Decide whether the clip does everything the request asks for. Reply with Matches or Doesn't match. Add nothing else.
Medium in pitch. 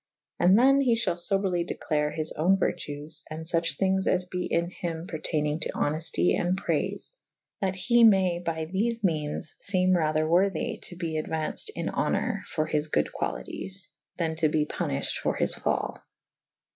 Matches